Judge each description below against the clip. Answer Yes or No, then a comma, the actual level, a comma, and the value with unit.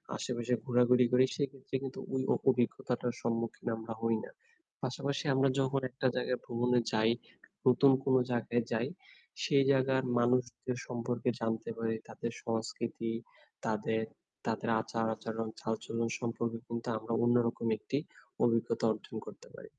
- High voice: No, low, 120 Hz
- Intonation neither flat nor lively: No, narrow, 1.9 semitones